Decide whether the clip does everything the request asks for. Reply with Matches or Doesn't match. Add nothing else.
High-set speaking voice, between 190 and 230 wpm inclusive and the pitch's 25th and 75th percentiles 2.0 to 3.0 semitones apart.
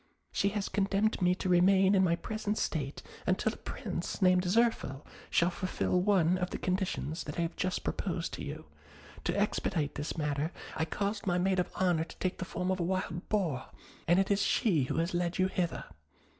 Doesn't match